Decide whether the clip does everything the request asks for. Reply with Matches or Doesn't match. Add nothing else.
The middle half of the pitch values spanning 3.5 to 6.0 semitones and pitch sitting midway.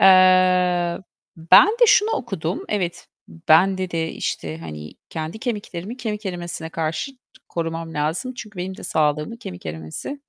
Matches